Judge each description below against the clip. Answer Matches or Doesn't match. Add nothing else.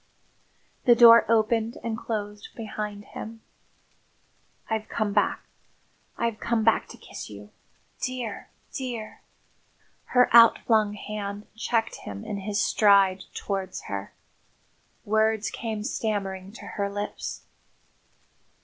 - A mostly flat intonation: Matches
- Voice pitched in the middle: Doesn't match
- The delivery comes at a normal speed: Doesn't match